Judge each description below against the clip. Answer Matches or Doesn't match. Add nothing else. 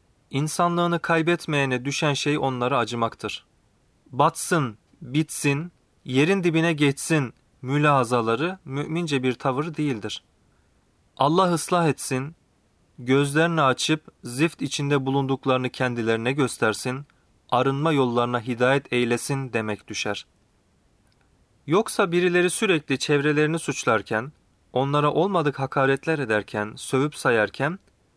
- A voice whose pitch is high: Doesn't match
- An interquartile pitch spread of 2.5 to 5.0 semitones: Matches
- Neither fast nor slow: Doesn't match